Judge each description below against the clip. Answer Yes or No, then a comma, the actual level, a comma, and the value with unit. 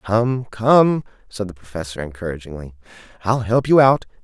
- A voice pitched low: Yes, low, 105 Hz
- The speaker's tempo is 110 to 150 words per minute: Yes, average, 140 wpm